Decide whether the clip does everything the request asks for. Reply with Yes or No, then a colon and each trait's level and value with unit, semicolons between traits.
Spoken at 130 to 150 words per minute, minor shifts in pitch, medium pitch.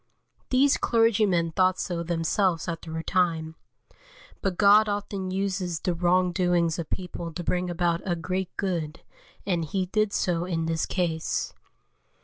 Yes: average, 145 wpm; narrow, 2.3 semitones; medium, 180 Hz